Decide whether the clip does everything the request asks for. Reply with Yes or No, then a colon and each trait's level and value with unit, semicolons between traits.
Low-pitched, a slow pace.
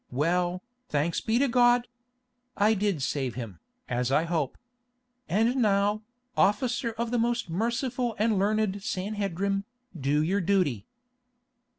No: high, 200 Hz; slow, 125 wpm